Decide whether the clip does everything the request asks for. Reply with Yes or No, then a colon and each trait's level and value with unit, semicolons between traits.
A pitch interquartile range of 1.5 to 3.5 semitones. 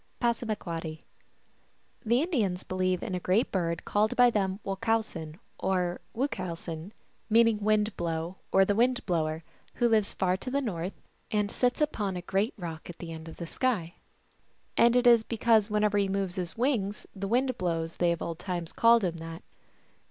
No: average, 4.7 semitones